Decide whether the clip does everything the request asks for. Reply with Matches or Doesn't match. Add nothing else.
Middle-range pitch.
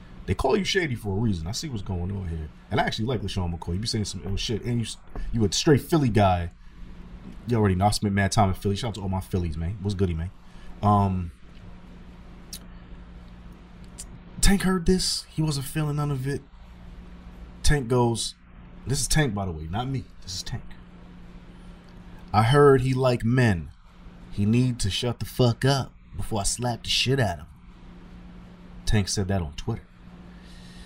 Doesn't match